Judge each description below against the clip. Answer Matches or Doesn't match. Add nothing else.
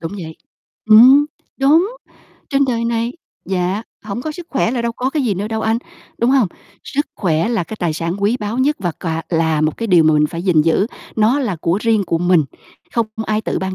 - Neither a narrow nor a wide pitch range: Doesn't match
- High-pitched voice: Matches